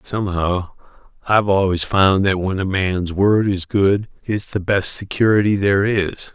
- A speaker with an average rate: Yes, average, 160 wpm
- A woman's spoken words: No, male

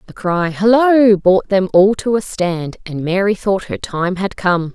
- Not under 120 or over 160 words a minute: No, average, 200 wpm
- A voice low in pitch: No, high, 195 Hz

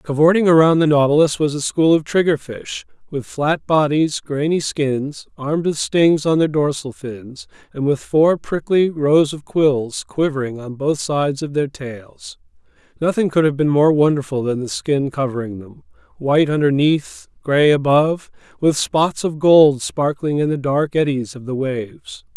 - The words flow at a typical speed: Yes, average, 165 wpm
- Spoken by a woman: No, male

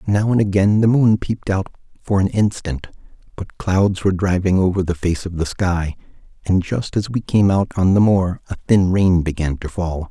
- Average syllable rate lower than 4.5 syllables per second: No, 5.0 syllables/s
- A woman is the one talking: No, male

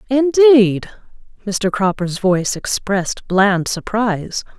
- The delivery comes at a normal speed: No, slow, 90 wpm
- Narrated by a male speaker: No, female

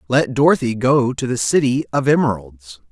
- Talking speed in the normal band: Yes, average, 165 wpm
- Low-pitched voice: Yes, low, 120 Hz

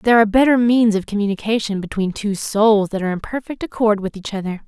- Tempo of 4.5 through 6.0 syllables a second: No, 6.3 syllables/s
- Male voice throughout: No, female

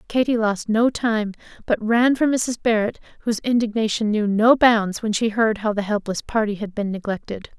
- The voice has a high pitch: Yes, high, 220 Hz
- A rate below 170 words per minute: No, average, 190 wpm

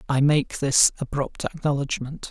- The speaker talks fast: No, slow, 130 wpm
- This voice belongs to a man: Yes, male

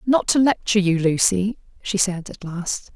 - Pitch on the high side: Yes, high, 195 Hz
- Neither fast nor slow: Yes, average, 185 wpm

